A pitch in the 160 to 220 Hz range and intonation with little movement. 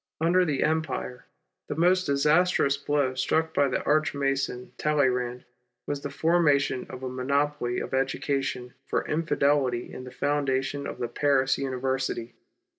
No: medium, 140 Hz; narrow, 2.3 semitones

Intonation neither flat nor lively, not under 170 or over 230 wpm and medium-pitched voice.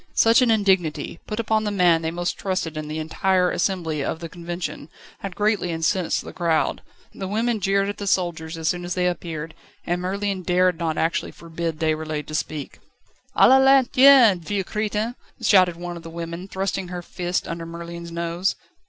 Yes: average, 3.0 semitones; average, 185 wpm; medium, 175 Hz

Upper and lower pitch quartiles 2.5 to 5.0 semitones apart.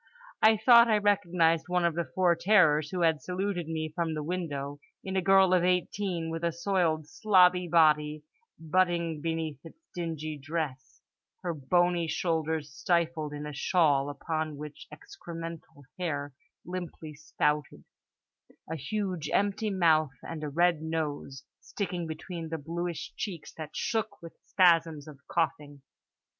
Yes: average, 2.9 semitones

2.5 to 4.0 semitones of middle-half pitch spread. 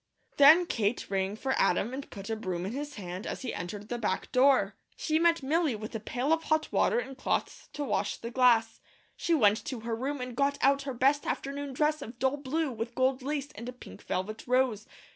No: average, 4.5 semitones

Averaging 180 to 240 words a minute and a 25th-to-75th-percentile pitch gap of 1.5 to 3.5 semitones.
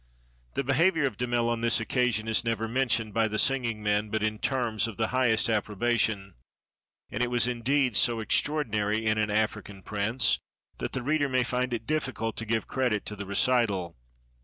Yes: average, 185 wpm; average, 2.7 semitones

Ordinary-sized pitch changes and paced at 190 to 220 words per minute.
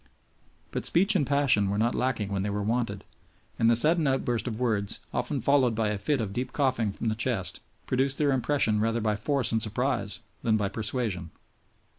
Yes: average, 4.0 semitones; average, 195 wpm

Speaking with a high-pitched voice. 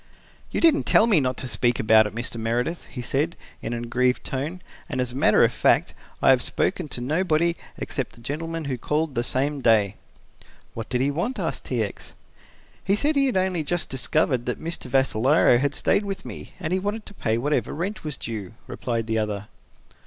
No: low, 135 Hz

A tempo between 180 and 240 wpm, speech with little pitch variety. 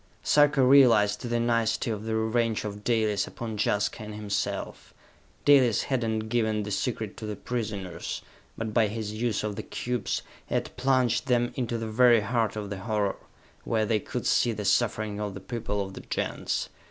Yes: average, 185 wpm; narrow, 2.2 semitones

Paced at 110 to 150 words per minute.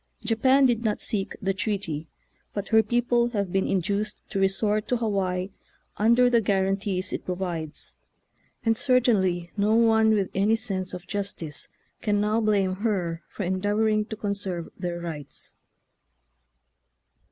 Yes: average, 140 wpm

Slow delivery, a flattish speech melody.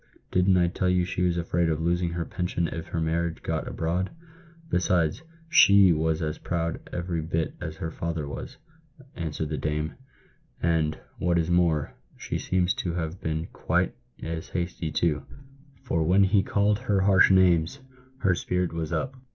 No: average, 170 wpm; narrow, 2.1 semitones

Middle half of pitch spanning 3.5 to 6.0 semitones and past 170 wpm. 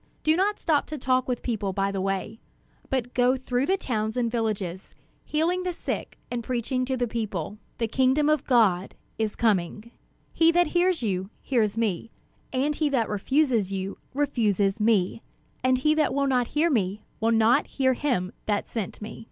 Yes: average, 4.9 semitones; average, 180 wpm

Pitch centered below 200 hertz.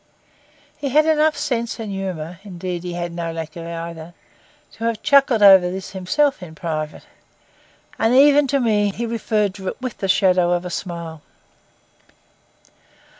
Yes: high, 190 Hz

